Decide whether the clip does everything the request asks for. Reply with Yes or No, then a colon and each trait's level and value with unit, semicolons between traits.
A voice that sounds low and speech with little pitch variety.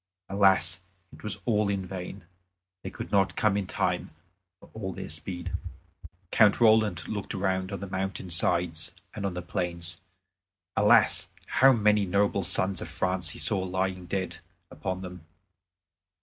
Yes: very low, 95 Hz; narrow, 1.9 semitones